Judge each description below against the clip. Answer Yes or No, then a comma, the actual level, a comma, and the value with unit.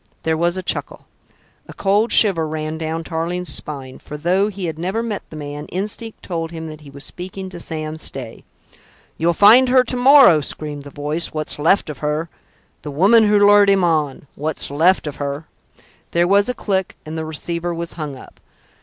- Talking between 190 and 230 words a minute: Yes, average, 195 wpm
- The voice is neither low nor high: Yes, medium, 165 Hz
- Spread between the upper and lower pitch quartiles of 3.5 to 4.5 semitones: Yes, average, 4.2 semitones